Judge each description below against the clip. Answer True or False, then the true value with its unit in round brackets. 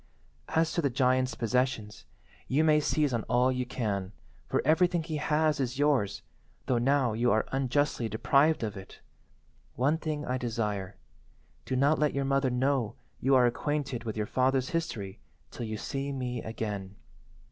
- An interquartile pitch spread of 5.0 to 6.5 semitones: False (4.0 semitones)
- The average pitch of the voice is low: True (130 Hz)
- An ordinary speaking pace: True (165 wpm)